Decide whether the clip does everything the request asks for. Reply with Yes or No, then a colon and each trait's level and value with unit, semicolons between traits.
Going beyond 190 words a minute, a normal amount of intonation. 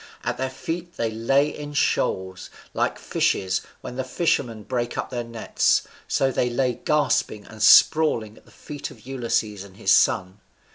No: average, 170 wpm; average, 4.1 semitones